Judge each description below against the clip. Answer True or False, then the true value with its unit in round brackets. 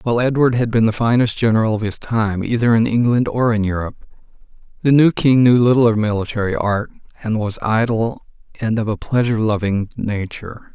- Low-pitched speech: True (115 Hz)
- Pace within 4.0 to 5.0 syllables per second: False (5.8 syllables/s)